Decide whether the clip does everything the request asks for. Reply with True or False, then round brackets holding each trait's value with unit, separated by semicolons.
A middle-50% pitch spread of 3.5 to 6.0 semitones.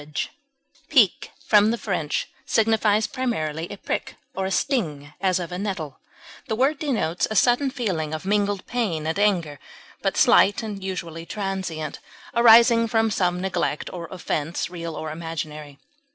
True (5.4 semitones)